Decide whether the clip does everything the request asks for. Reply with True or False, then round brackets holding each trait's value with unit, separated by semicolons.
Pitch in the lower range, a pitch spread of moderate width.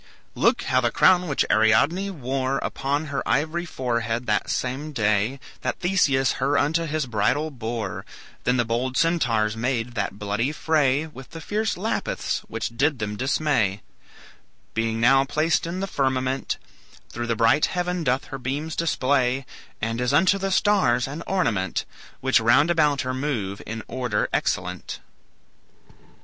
True (130 Hz; 4.9 semitones)